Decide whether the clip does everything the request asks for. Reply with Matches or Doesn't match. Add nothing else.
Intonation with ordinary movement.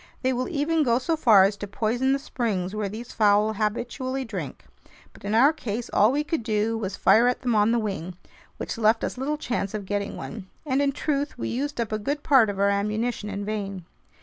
Matches